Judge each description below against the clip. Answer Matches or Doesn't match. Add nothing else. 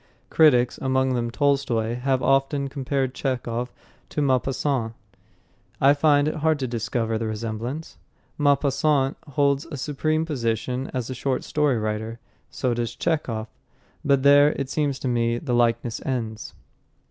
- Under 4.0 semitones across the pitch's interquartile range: Matches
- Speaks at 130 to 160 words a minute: Matches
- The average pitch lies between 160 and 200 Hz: Doesn't match